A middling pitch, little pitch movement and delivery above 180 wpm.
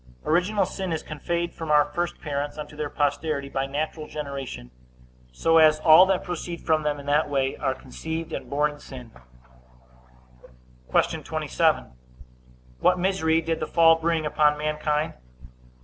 No: medium, 155 Hz; narrow, 2.1 semitones; average, 150 wpm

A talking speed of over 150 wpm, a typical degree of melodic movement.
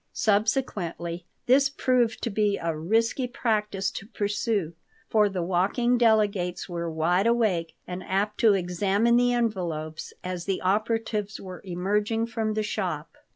No: average, 140 wpm; average, 3.9 semitones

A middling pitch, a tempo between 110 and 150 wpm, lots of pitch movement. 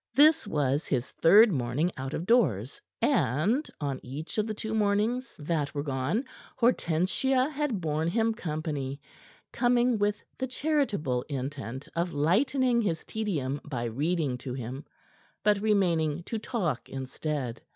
Yes: medium, 165 Hz; average, 140 wpm; wide, 8.1 semitones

